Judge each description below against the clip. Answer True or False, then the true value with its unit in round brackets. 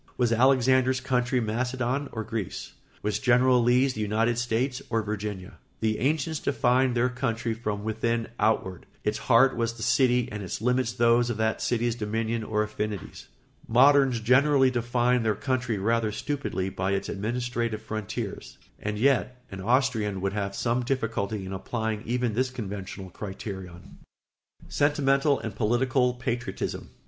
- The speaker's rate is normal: True (150 wpm)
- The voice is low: True (115 Hz)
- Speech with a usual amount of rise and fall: True (3.0 semitones)